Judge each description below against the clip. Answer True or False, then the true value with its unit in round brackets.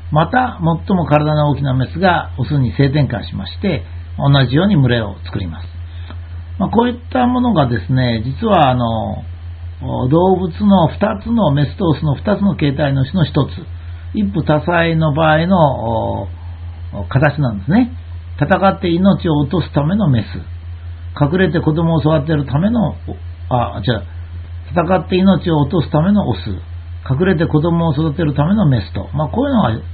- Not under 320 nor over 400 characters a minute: False (295 characters per minute)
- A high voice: False (140 Hz)